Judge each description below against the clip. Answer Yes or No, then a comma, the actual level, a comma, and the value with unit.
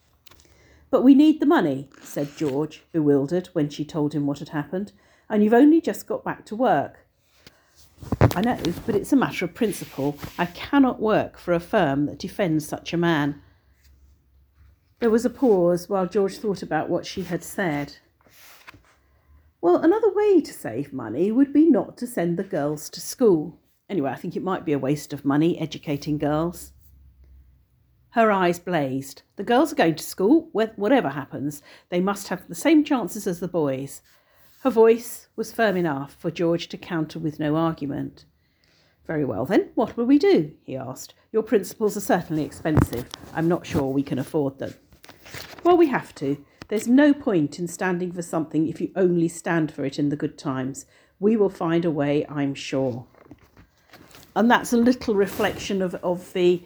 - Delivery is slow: No, average, 180 wpm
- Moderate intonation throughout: No, wide, 7.0 semitones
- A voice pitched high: No, medium, 170 Hz